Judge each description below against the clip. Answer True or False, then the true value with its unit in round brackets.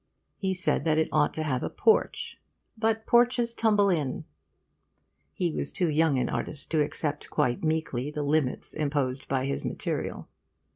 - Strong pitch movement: False (5.0 semitones)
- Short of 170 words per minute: True (160 wpm)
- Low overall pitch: False (155 Hz)